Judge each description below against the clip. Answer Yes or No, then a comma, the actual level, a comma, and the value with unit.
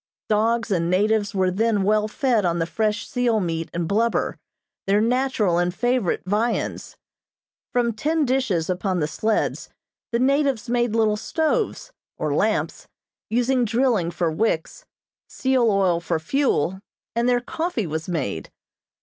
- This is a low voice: No, high, 215 Hz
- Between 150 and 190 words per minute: No, average, 140 wpm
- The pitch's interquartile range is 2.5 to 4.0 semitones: No, average, 5.2 semitones